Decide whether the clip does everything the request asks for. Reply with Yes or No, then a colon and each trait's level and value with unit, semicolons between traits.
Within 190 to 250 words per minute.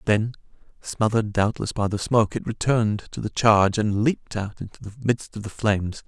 Yes: average, 200 wpm